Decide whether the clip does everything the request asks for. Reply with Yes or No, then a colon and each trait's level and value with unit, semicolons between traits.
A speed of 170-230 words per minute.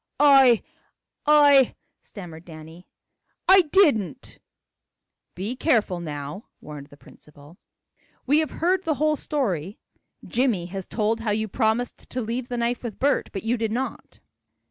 No: average, 145 wpm